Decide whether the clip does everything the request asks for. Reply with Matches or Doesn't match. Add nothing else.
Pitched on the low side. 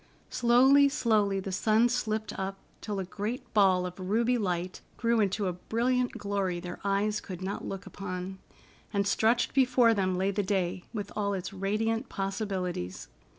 Doesn't match